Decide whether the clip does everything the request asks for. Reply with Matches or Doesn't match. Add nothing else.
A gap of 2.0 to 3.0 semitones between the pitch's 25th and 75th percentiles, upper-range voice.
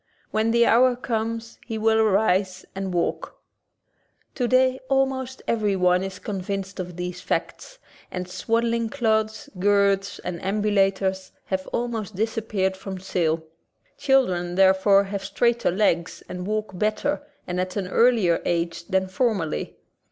Doesn't match